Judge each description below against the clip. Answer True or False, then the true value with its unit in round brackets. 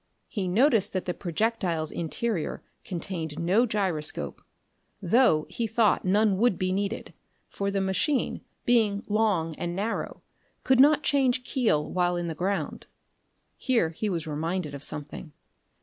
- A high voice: True (195 Hz)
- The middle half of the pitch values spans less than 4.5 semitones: False (5.0 semitones)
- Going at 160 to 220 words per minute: False (140 wpm)